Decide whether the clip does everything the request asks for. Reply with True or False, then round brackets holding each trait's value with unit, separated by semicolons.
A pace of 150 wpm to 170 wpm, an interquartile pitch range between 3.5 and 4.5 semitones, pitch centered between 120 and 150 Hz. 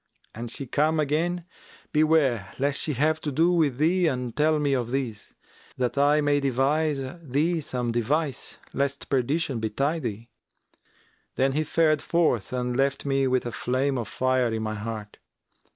True (165 wpm; 3.9 semitones; 135 Hz)